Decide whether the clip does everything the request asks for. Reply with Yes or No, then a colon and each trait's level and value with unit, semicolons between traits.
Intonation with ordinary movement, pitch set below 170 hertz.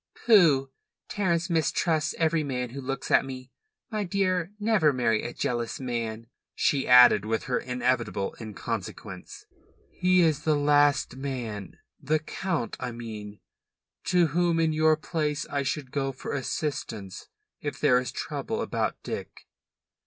Yes: average, 4.5 semitones; medium, 140 Hz